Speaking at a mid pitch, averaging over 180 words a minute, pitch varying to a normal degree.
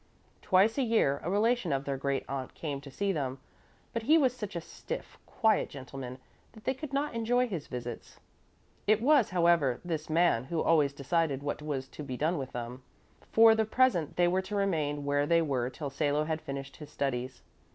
No: medium, 155 Hz; average, 200 wpm; wide, 7.2 semitones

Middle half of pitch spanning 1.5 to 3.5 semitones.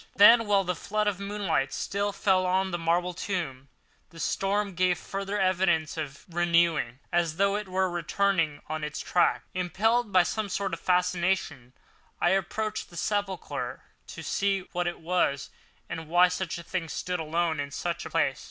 Yes: average, 2.9 semitones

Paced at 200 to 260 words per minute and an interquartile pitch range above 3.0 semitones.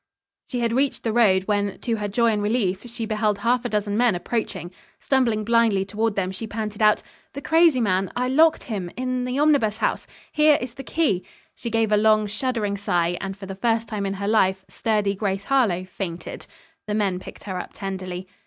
Yes: fast, 205 wpm; average, 3.5 semitones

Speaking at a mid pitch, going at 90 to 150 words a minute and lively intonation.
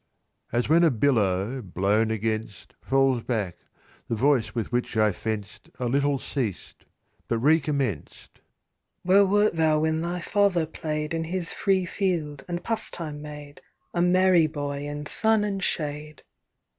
Yes: medium, 145 Hz; average, 145 wpm; wide, 6.2 semitones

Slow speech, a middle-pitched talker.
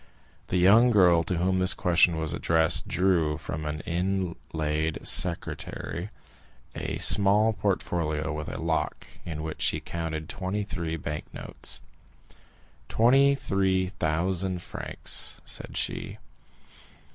No: slow, 120 wpm; very low, 85 Hz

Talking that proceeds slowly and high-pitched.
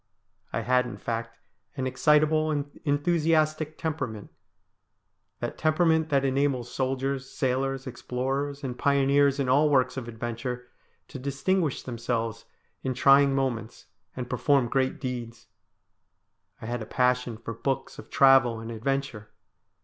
No: slow, 130 wpm; low, 135 Hz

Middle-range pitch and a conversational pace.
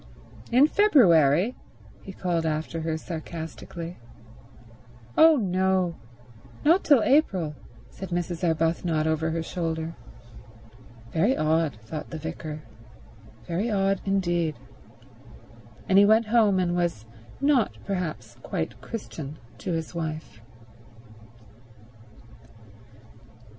No: medium, 170 Hz; slow, 95 wpm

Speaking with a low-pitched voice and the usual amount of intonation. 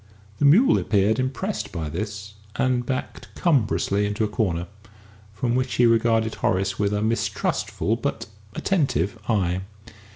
Yes: low, 110 Hz; average, 4.0 semitones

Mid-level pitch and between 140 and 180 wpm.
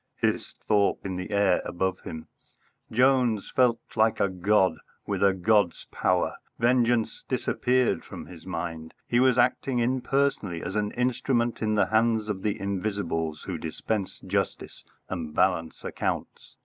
No: low, 105 Hz; average, 145 wpm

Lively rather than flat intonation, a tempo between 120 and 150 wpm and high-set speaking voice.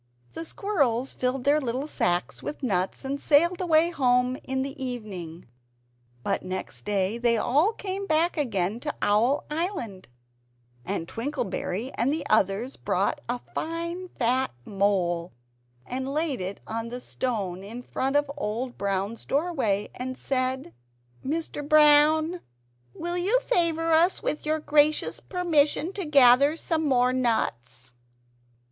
Yes: wide, 5.8 semitones; slow, 135 wpm; very high, 265 Hz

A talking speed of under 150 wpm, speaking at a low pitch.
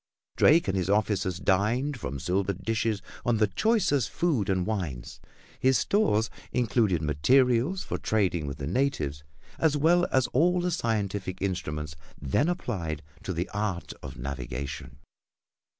Yes: average, 140 wpm; low, 100 Hz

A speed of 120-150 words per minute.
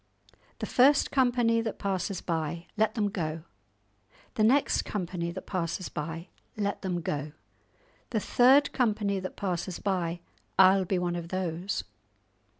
Yes: average, 140 wpm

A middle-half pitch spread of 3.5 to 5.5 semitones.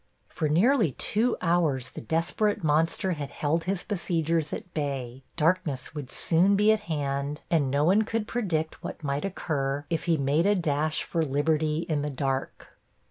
Yes: average, 3.8 semitones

